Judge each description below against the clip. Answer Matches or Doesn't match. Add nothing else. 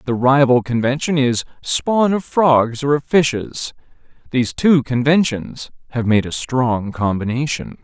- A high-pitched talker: Doesn't match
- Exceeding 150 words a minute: Doesn't match